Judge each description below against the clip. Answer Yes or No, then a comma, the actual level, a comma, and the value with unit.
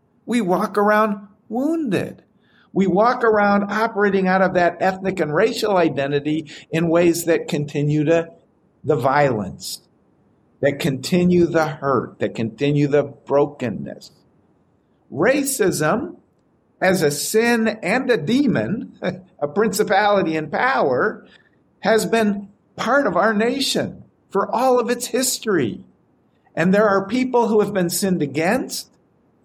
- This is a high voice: Yes, high, 195 Hz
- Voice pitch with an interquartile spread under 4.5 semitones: No, wide, 5.6 semitones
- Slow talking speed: Yes, slow, 125 wpm